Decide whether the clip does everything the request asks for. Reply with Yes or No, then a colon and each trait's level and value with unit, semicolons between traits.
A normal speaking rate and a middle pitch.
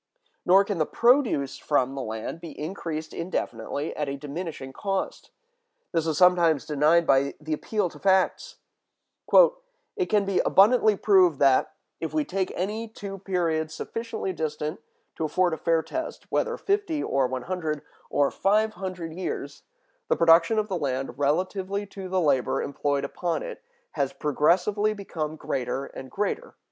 Yes: average, 155 wpm; medium, 170 Hz